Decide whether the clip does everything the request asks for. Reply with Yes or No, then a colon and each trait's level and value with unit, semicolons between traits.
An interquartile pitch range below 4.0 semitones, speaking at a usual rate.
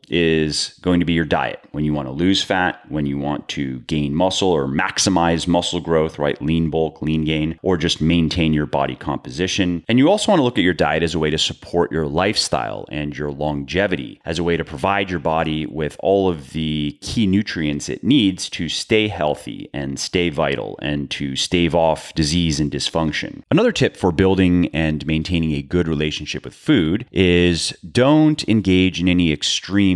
Yes: average, 2.9 semitones; average, 195 wpm